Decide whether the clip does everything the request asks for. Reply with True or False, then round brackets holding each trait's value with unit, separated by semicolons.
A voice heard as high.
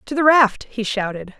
True (235 Hz)